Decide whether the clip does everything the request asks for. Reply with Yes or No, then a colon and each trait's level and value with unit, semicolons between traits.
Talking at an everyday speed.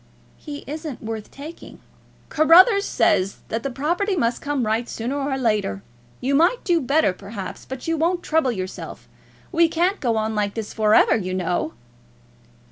Yes: average, 165 wpm